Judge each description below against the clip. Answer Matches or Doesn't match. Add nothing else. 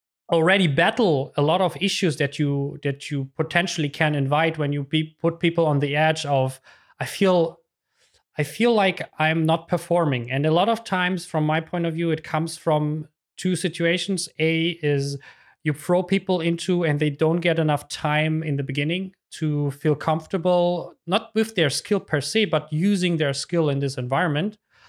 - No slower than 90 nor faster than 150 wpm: Doesn't match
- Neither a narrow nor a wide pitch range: Matches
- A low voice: Doesn't match